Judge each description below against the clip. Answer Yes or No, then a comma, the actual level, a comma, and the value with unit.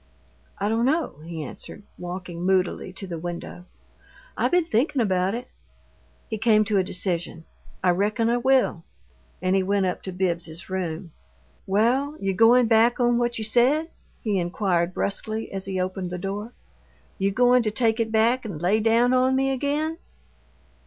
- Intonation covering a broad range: No, average, 4.6 semitones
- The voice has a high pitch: Yes, high, 210 Hz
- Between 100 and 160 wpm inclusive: No, average, 170 wpm